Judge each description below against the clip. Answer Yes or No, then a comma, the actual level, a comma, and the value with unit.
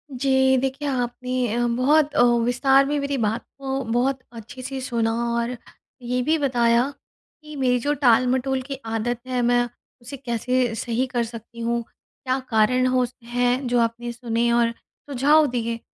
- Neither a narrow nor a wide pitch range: No, narrow, 2.1 semitones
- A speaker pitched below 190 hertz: No, very high, 250 Hz